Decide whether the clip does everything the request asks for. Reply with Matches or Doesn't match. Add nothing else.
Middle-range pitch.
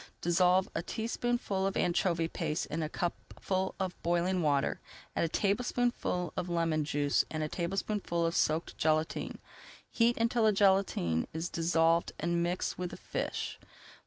Matches